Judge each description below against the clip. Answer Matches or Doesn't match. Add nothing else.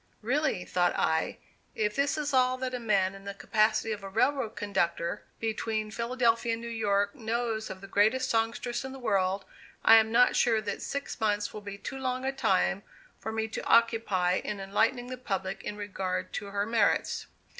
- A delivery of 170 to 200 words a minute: Matches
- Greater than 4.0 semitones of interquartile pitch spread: Doesn't match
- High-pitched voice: Matches